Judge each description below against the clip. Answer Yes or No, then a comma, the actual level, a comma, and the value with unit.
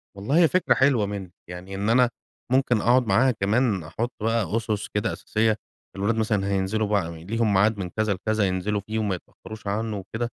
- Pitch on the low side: Yes, low, 105 Hz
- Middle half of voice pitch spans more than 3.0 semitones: No, narrow, 2.6 semitones